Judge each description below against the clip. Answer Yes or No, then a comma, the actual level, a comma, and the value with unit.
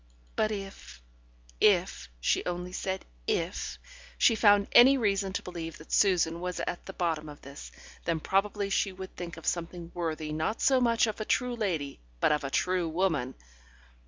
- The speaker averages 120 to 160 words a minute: No, average, 175 wpm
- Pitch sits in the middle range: Yes, medium, 180 Hz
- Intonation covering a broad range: No, average, 3.7 semitones